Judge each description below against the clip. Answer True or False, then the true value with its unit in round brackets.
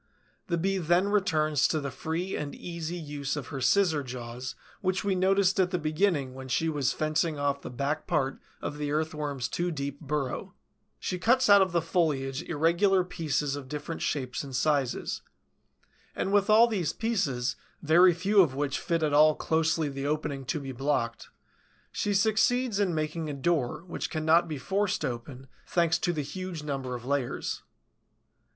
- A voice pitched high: False (155 Hz)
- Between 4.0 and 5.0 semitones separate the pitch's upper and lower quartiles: True (4.3 semitones)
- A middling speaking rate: True (175 wpm)